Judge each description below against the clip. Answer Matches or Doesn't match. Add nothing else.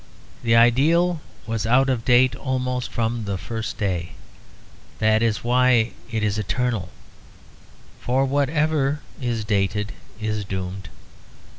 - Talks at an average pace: Doesn't match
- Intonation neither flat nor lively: Matches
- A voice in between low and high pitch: Doesn't match